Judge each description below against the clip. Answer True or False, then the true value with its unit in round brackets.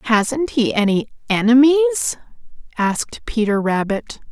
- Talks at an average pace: False (95 wpm)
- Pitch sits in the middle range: False (245 Hz)